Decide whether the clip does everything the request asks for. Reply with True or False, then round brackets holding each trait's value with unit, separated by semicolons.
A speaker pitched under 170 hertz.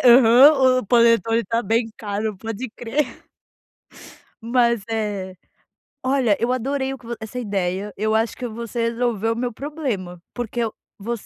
False (230 Hz)